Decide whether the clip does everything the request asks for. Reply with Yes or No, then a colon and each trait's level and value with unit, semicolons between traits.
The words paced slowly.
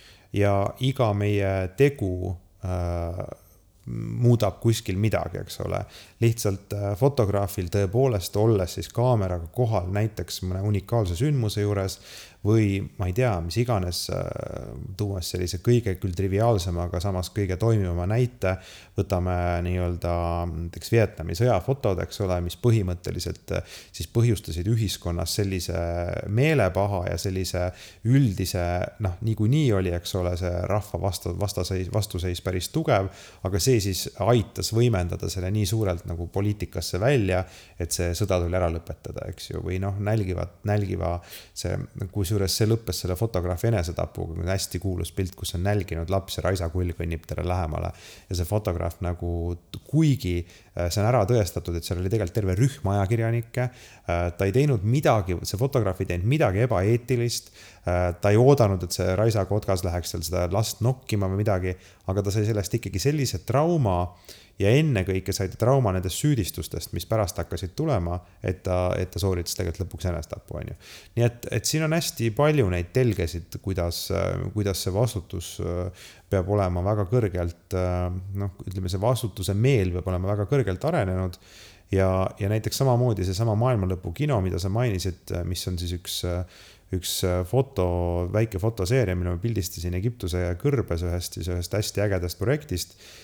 No: average, 150 wpm